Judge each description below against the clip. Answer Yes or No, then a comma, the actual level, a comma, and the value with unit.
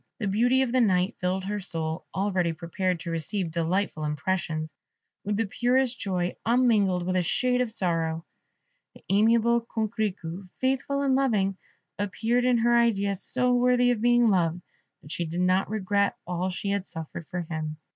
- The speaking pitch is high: Yes, high, 195 Hz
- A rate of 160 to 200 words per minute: Yes, average, 165 wpm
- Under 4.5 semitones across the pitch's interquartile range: No, average, 5.1 semitones